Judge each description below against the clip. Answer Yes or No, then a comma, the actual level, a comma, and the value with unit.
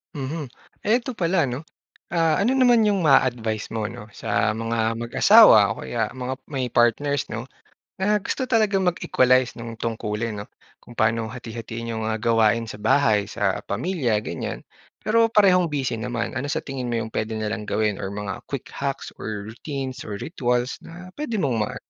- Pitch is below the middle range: Yes, low, 120 Hz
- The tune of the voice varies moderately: No, wide, 6.6 semitones